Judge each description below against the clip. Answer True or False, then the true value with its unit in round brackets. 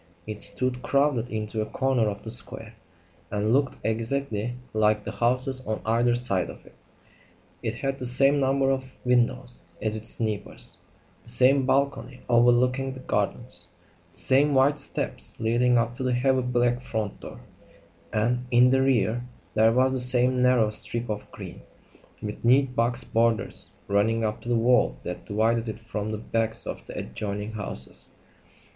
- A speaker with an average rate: True (165 wpm)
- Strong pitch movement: False (2.8 semitones)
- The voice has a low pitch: True (120 Hz)